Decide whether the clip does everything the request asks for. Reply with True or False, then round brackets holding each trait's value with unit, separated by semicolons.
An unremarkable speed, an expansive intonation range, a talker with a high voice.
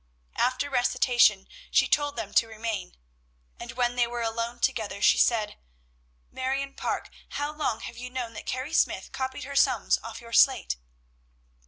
False (160 wpm; 2.5 semitones; 245 Hz)